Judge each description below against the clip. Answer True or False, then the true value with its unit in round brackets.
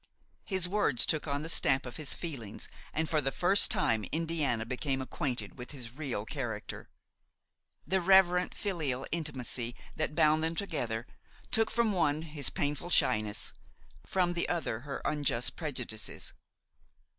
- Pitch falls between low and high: True (150 Hz)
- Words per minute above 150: False (145 wpm)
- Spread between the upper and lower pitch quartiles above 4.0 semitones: True (5.3 semitones)